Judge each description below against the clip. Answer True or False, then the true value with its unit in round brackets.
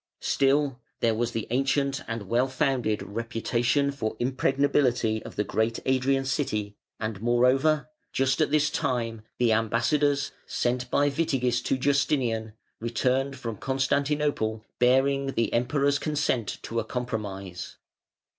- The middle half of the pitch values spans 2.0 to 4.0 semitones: True (3.3 semitones)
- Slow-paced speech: True (125 wpm)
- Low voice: True (125 Hz)